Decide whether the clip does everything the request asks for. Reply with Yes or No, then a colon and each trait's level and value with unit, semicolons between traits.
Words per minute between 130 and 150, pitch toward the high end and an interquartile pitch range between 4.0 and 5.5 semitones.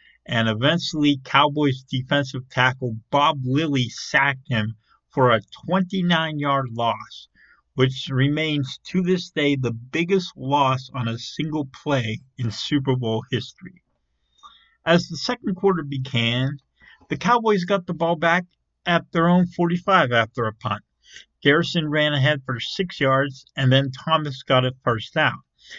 No: average, 140 wpm; medium, 140 Hz; average, 4.6 semitones